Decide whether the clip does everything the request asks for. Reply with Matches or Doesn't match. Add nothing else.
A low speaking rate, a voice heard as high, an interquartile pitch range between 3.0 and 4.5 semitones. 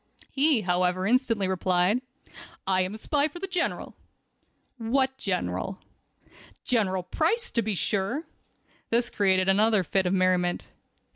Doesn't match